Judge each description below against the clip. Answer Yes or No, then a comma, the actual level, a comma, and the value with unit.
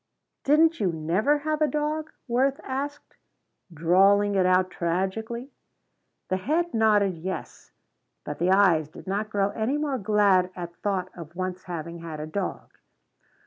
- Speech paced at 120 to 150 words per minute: Yes, average, 145 wpm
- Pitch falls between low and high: No, high, 200 Hz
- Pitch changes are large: Yes, wide, 6.6 semitones